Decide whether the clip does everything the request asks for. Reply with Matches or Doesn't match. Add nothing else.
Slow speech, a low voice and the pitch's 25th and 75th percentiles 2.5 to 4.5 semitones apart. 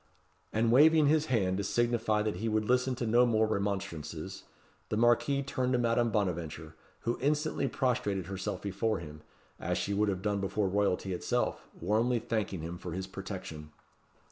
Doesn't match